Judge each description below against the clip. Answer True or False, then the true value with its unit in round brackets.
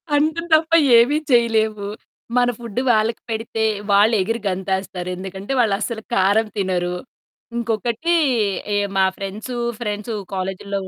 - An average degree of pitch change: True (3.3 semitones)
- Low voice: False (215 Hz)